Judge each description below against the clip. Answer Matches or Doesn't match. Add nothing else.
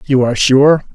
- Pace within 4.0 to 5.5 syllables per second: Matches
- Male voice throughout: Matches